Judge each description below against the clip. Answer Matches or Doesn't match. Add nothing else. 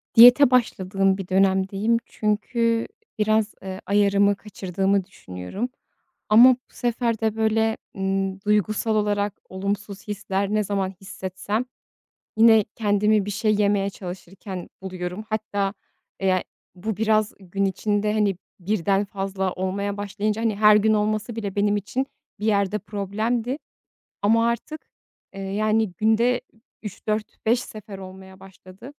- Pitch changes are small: Matches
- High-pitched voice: Matches